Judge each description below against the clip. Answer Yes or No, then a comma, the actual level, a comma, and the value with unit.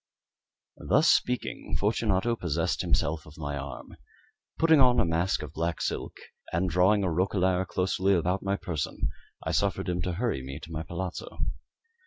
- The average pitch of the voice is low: Yes, very low, 90 Hz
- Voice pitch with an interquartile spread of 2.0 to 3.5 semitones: Yes, average, 3.1 semitones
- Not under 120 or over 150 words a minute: No, average, 160 wpm